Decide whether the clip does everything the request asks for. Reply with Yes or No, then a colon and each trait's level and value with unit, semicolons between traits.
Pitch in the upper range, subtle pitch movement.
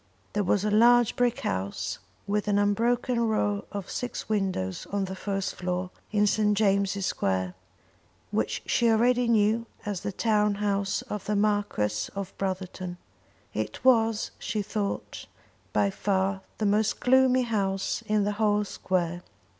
Yes: high, 205 Hz; narrow, 2.2 semitones